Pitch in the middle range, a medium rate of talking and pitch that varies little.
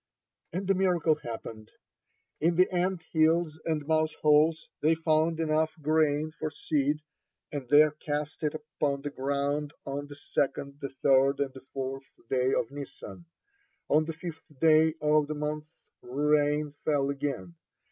Yes: medium, 150 Hz; average, 150 wpm; narrow, 2.0 semitones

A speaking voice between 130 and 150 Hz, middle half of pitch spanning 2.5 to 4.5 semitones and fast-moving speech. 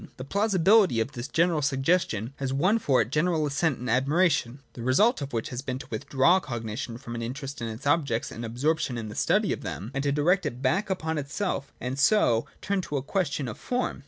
No: medium, 140 Hz; wide, 5.5 semitones; fast, 220 wpm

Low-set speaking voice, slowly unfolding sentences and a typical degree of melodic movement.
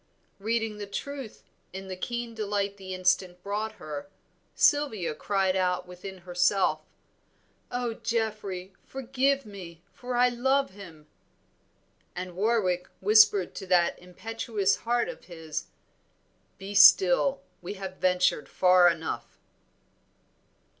No: high, 195 Hz; slow, 115 wpm; average, 3.8 semitones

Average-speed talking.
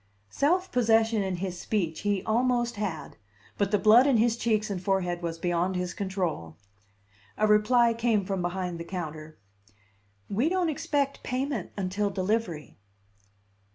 Yes: average, 145 wpm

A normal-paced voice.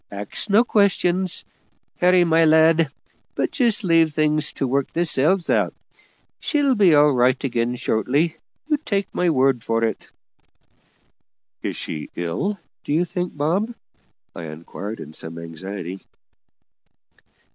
No: slow, 130 wpm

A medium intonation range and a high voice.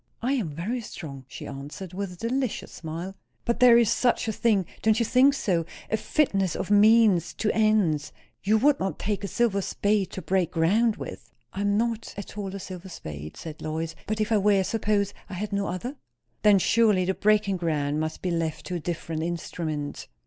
Yes: average, 4.4 semitones; high, 195 Hz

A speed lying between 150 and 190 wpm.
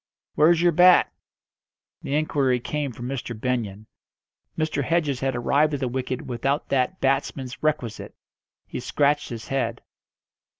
No: slow, 135 wpm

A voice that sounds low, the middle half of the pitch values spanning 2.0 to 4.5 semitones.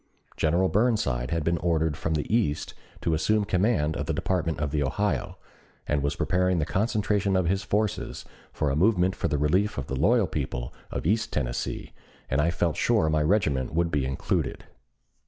No: very low, 85 Hz; average, 4.9 semitones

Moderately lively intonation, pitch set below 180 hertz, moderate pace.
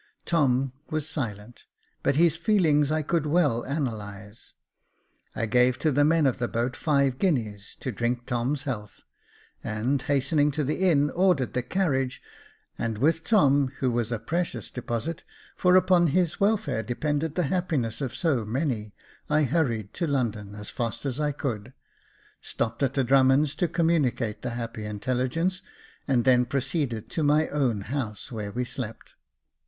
Yes: average, 4.7 semitones; low, 135 Hz; average, 160 wpm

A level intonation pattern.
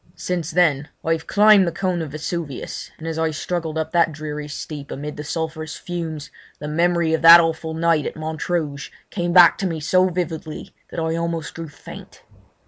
Yes: narrow, 1.9 semitones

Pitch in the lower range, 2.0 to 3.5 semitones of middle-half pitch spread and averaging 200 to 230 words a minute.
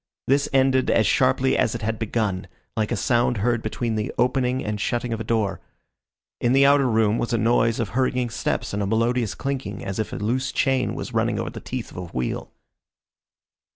Yes: low, 120 Hz; average, 2.9 semitones; fast, 205 wpm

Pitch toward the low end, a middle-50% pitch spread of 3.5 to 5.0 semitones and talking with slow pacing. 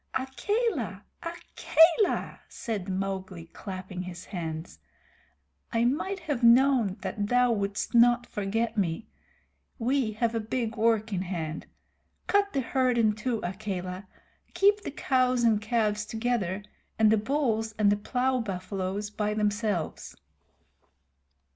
No: high, 220 Hz; average, 4.2 semitones; slow, 125 wpm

